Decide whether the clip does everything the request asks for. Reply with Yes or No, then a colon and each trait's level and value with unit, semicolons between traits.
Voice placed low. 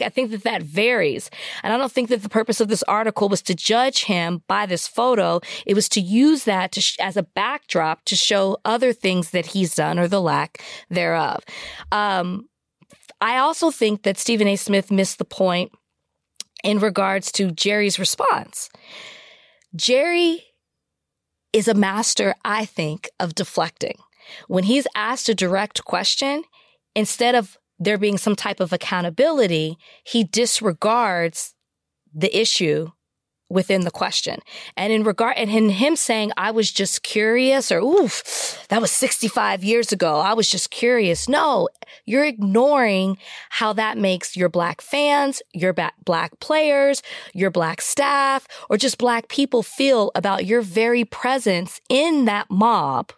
No: high, 215 Hz